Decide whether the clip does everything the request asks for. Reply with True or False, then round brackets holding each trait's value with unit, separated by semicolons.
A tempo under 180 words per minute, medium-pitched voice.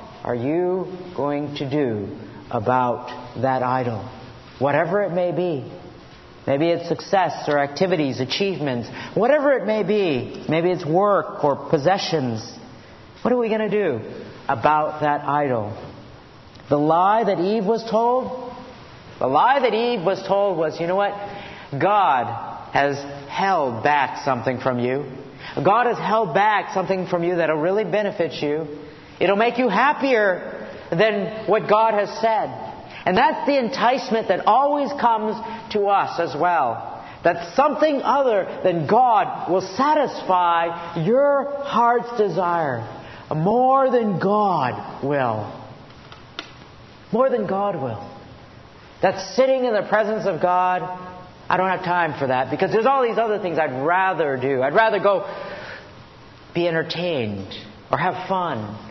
True (140 wpm; 180 Hz)